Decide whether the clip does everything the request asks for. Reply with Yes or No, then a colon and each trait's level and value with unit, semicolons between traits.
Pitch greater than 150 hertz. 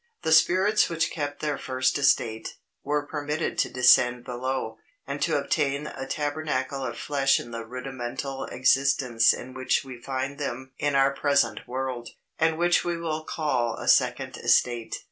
No: low, 135 Hz